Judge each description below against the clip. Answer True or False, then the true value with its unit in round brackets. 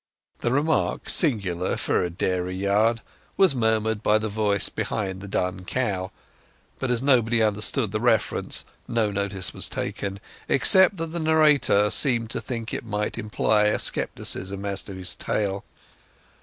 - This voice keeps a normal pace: True (150 wpm)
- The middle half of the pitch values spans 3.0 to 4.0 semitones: True (3.5 semitones)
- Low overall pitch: True (105 Hz)